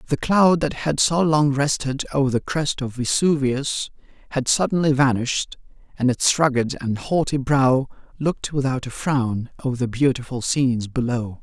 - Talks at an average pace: Yes, average, 160 wpm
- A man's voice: Yes, male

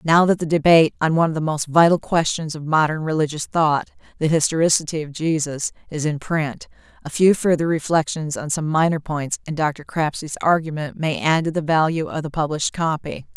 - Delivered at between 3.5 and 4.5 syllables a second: No, 5.5 syllables/s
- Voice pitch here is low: No, medium, 155 Hz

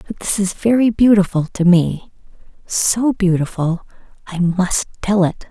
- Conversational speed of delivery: No, slow, 130 wpm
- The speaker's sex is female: Yes, female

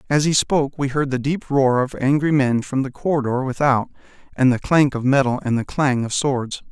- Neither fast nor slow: No, fast, 225 wpm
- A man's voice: Yes, male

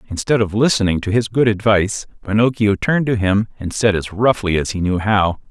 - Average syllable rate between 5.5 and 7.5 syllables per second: Yes, 5.7 syllables/s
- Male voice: Yes, male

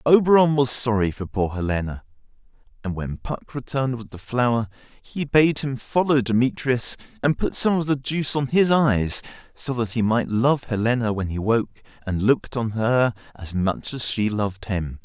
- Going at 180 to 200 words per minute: Yes, average, 185 wpm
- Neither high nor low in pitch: No, low, 120 Hz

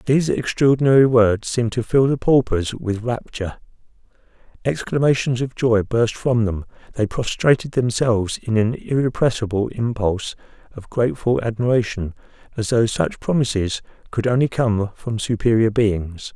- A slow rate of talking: Yes, slow, 130 wpm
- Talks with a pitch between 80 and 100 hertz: No, low, 115 Hz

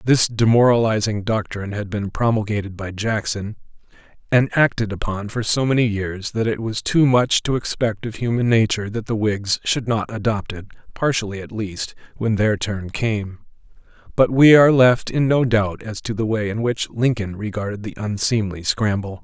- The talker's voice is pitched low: Yes, low, 110 Hz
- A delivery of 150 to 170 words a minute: No, average, 180 wpm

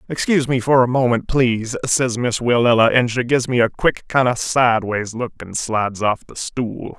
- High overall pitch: No, low, 120 Hz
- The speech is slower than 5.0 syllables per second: No, 5.1 syllables/s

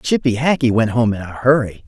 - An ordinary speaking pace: No, fast, 225 wpm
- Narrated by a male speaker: Yes, male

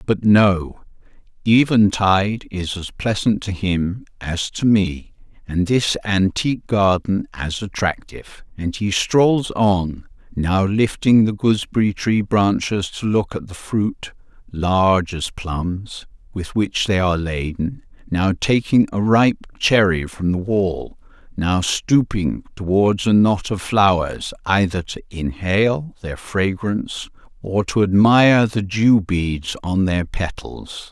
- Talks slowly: Yes, slow, 130 wpm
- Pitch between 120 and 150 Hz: No, low, 100 Hz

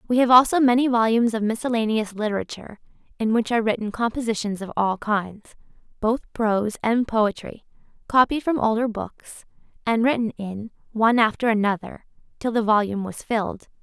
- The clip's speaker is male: No, female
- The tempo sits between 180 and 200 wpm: No, average, 150 wpm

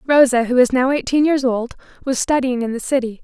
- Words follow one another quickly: Yes, fast, 220 wpm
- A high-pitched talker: Yes, very high, 255 Hz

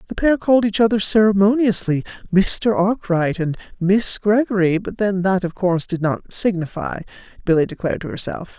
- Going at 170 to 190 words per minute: No, average, 155 wpm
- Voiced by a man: No, female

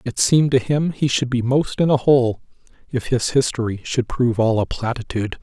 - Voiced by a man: Yes, male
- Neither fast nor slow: No, fast, 210 wpm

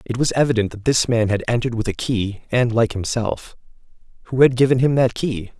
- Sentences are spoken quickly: Yes, fast, 215 wpm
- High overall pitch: No, low, 120 Hz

